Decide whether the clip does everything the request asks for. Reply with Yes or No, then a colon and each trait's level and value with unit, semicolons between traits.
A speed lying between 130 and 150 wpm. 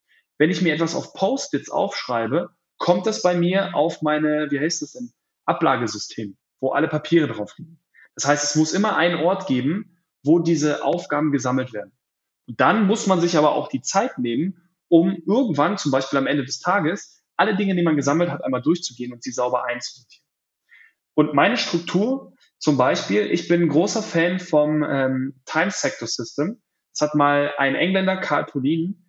No: average, 175 wpm